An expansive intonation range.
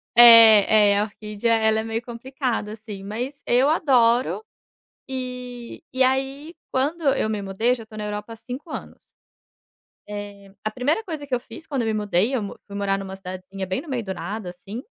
No: average, 3.9 semitones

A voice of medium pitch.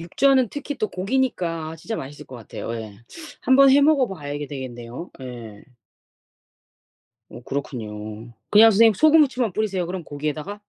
Yes: medium, 175 Hz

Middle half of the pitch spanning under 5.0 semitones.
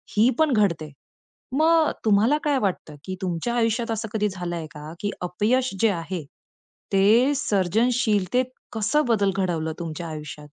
No: wide, 5.4 semitones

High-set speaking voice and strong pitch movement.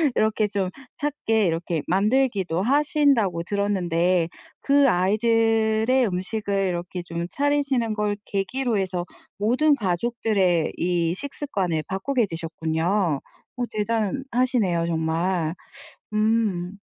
No: high, 200 Hz; average, 4.8 semitones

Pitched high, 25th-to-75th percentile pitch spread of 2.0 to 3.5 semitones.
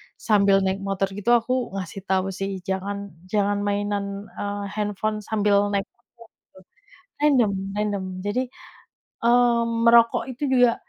Yes: high, 205 Hz; average, 2.8 semitones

